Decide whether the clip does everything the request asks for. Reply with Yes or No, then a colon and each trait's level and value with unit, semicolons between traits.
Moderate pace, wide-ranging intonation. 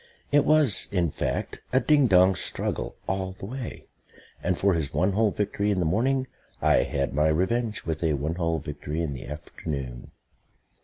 Yes: average, 175 wpm; wide, 5.7 semitones